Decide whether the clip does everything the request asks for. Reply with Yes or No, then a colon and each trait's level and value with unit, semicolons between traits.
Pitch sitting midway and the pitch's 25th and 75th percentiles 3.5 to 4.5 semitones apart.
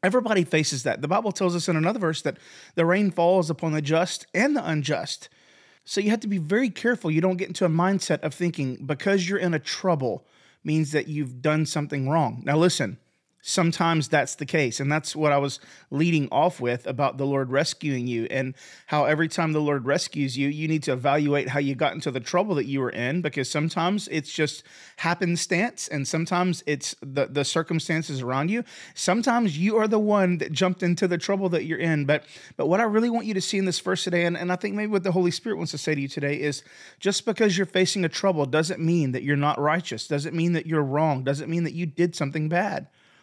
Yes: medium, 160 Hz; average, 3.8 semitones